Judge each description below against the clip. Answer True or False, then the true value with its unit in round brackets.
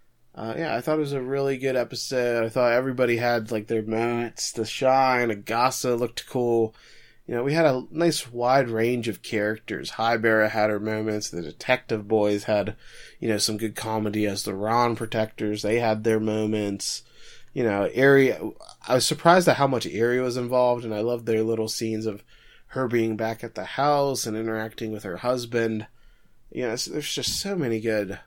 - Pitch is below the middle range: True (115 Hz)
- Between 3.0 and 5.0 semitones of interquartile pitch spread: False (2.4 semitones)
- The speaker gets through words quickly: False (195 wpm)